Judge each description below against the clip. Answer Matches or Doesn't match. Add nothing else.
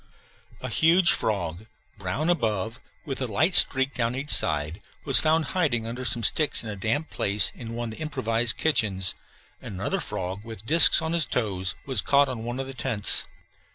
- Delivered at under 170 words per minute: Doesn't match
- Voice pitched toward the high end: Doesn't match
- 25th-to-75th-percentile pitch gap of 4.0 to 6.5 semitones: Matches